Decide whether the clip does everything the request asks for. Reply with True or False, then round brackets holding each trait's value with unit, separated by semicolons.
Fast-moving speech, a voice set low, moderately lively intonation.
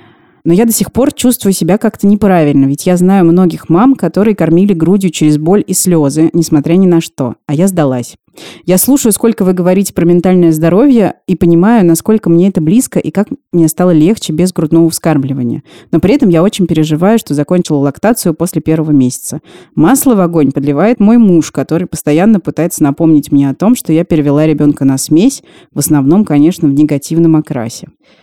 False (185 wpm; 170 Hz; 4.1 semitones)